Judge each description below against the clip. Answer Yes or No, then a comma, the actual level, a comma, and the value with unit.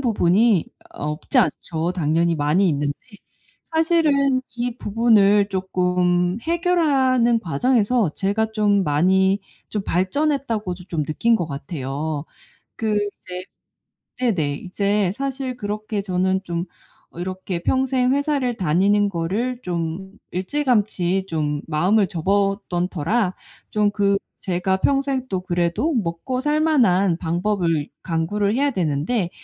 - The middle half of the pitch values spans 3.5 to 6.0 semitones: Yes, wide, 5.5 semitones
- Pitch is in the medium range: No, high, 195 Hz